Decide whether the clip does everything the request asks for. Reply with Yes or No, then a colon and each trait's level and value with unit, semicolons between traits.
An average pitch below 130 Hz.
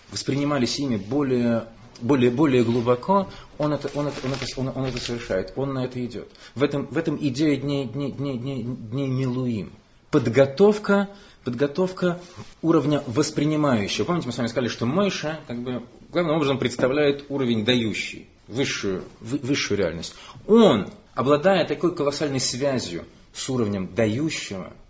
No: low, 135 Hz